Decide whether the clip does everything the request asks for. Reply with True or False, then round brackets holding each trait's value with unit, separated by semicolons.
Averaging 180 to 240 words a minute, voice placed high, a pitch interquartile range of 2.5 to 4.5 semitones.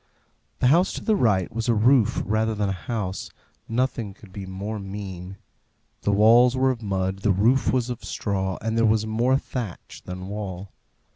False (185 wpm; 105 Hz; 3.6 semitones)